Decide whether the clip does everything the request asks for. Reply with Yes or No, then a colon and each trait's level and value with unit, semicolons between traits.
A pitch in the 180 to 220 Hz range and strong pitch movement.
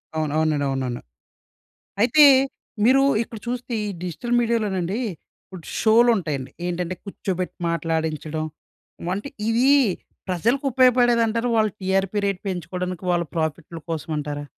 Yes: medium, 185 Hz; wide, 6.3 semitones